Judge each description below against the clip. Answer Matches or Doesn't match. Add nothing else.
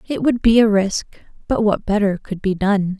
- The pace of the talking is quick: Matches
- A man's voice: Doesn't match